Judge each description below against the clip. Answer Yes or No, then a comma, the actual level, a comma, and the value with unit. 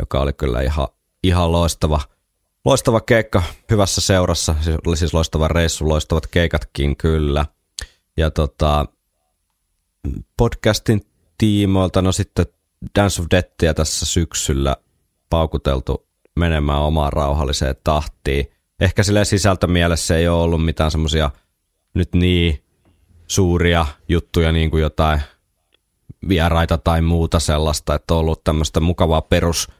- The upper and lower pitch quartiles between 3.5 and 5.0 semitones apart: No, narrow, 2.5 semitones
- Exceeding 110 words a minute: Yes, average, 120 wpm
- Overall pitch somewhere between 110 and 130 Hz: No, very low, 80 Hz